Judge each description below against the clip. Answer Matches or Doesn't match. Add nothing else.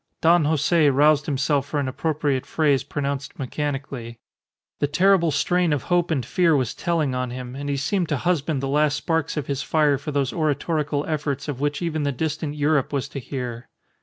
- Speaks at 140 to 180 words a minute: Doesn't match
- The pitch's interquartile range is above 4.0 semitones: Doesn't match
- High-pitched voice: Doesn't match